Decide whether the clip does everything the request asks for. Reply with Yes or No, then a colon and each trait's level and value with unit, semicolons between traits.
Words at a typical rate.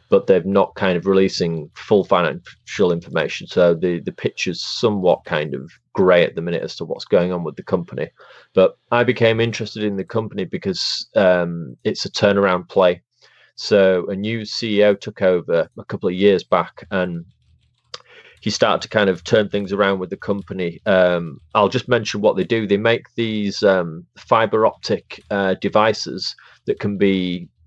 Yes: average, 180 wpm